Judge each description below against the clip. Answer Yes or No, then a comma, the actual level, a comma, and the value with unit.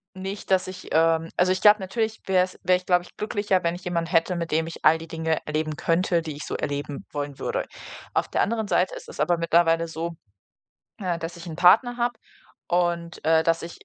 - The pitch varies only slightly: Yes, narrow, 2.3 semitones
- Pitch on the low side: No, medium, 170 Hz